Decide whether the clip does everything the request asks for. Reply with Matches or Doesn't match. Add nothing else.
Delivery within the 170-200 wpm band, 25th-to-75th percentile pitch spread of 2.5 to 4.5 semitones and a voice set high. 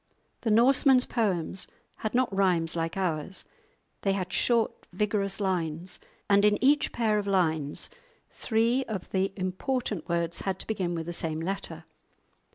Doesn't match